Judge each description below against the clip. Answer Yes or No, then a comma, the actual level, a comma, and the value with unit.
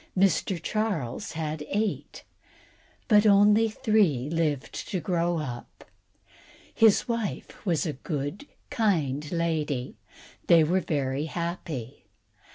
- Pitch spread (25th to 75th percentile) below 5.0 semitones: No, wide, 5.5 semitones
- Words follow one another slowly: Yes, slow, 110 wpm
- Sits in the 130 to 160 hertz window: No, medium, 170 Hz